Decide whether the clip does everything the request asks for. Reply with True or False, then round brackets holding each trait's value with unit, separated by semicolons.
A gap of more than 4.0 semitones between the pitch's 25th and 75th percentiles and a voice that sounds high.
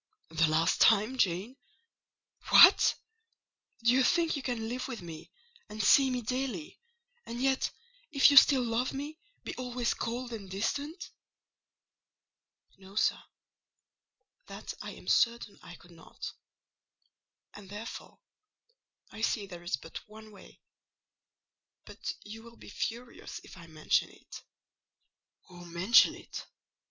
True (5.2 semitones; 225 Hz)